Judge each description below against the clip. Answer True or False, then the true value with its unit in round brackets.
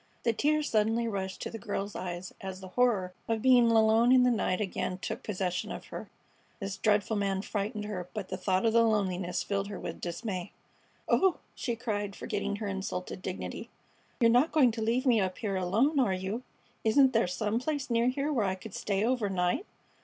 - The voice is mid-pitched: False (210 Hz)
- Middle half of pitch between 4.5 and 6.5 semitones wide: False (3.7 semitones)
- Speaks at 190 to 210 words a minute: True (200 wpm)